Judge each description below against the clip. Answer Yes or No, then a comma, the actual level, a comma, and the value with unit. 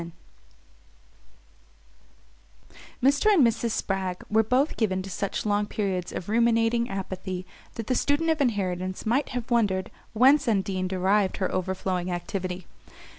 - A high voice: Yes, high, 205 Hz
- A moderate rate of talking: No, slow, 130 wpm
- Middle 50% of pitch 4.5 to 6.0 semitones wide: No, average, 4.1 semitones